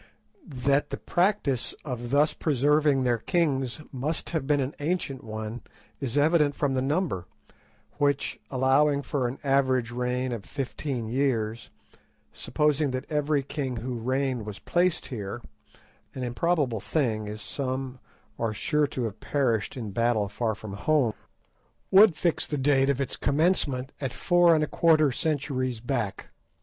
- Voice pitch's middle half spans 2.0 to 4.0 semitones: Yes, average, 3.6 semitones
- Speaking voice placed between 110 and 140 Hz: Yes, low, 135 Hz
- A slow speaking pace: No, average, 145 wpm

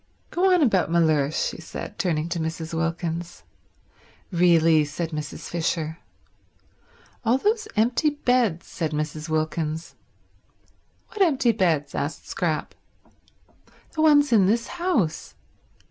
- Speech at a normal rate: No, slow, 115 wpm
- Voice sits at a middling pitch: Yes, medium, 170 Hz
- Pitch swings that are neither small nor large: No, wide, 7.1 semitones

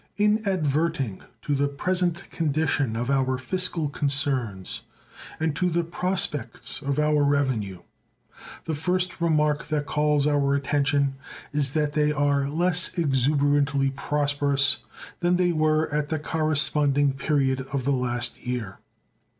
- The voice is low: No, medium, 145 Hz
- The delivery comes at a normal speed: No, slow, 130 wpm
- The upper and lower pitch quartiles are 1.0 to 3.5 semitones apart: Yes, narrow, 2.4 semitones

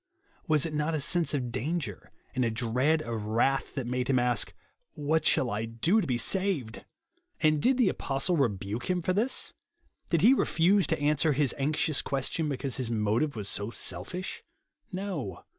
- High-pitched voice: No, medium, 140 Hz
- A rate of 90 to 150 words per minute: No, average, 185 wpm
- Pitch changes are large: Yes, wide, 5.9 semitones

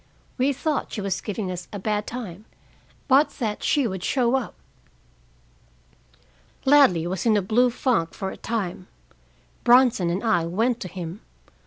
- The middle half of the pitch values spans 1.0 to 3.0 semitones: No, average, 5.1 semitones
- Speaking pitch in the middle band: No, high, 215 Hz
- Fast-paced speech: No, average, 155 wpm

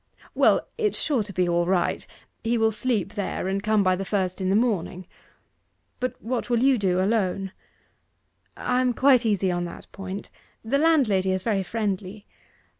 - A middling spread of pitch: Yes, average, 4.0 semitones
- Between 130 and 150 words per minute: No, average, 175 wpm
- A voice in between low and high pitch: No, high, 205 Hz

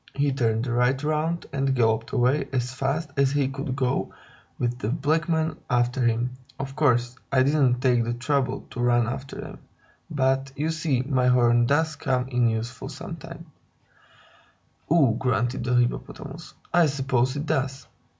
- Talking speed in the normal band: Yes, average, 160 wpm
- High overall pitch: No, low, 130 Hz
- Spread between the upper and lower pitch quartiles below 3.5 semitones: Yes, narrow, 2.5 semitones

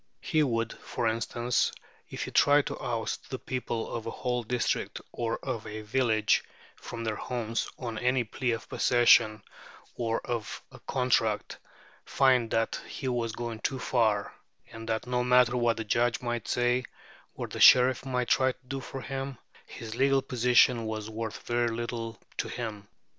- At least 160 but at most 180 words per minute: Yes, average, 170 wpm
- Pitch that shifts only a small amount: Yes, narrow, 1.8 semitones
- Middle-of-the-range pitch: No, low, 120 Hz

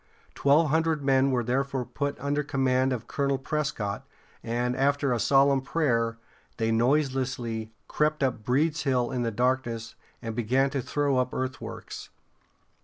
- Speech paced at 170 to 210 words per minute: No, average, 145 wpm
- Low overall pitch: Yes, low, 130 Hz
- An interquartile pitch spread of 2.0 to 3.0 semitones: Yes, average, 2.7 semitones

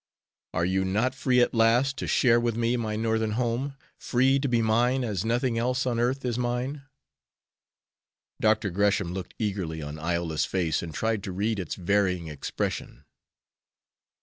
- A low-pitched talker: Yes, low, 110 Hz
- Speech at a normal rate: Yes, average, 160 wpm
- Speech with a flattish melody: No, average, 4.5 semitones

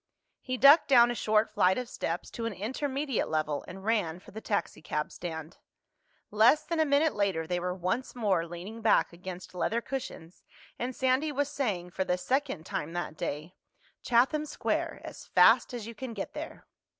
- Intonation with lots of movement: Yes, wide, 6.5 semitones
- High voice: Yes, high, 215 Hz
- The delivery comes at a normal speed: Yes, average, 175 wpm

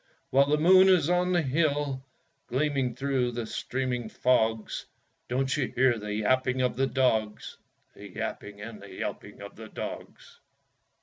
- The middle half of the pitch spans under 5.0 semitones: Yes, average, 3.6 semitones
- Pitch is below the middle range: Yes, low, 130 Hz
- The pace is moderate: Yes, average, 150 wpm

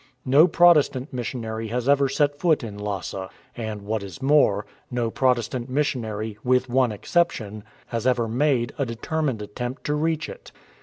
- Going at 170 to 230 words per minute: No, average, 155 wpm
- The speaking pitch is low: Yes, low, 125 Hz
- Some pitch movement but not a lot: Yes, average, 4.3 semitones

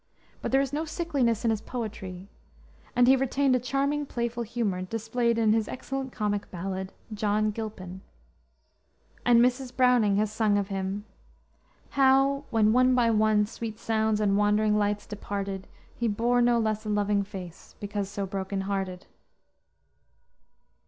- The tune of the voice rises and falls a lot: No, average, 3.2 semitones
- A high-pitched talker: Yes, high, 215 Hz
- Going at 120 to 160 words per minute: Yes, average, 150 wpm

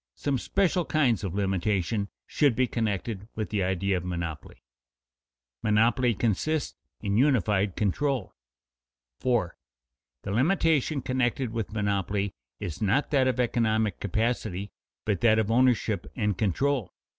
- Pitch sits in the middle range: No, low, 110 Hz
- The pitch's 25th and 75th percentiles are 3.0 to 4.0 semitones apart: No, average, 4.4 semitones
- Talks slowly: Yes, slow, 130 wpm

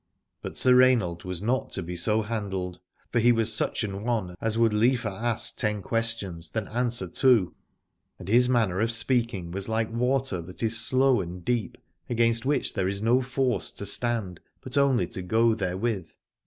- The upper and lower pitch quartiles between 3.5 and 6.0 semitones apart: Yes, average, 4.0 semitones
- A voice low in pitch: Yes, low, 115 Hz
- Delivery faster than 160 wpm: Yes, average, 180 wpm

